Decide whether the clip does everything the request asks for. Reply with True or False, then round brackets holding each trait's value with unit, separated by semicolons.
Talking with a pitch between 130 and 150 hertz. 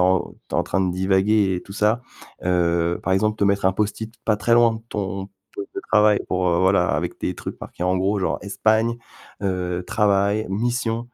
False (100 Hz)